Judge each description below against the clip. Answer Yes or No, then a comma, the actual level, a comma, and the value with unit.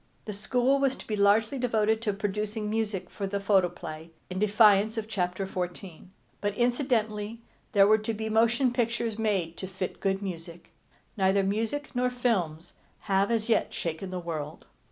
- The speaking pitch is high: Yes, high, 210 Hz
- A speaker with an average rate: Yes, average, 165 wpm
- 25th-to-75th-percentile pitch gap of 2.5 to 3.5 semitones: Yes, average, 2.9 semitones